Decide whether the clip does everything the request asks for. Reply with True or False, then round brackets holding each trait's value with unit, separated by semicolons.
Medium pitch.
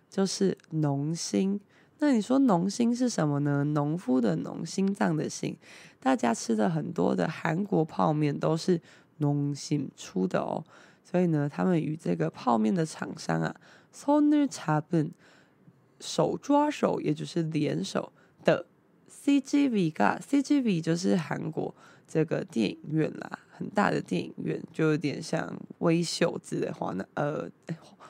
True (170 Hz)